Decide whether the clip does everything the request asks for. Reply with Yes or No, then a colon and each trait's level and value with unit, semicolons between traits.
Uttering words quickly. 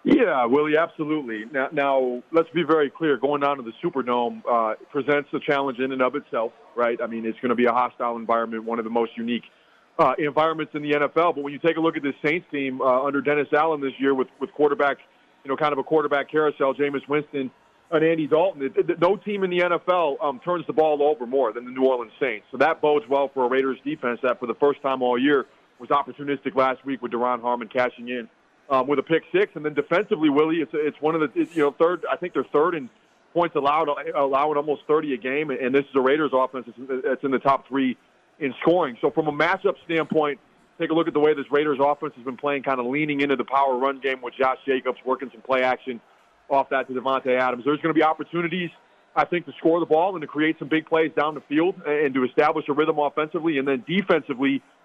Yes: fast, 245 wpm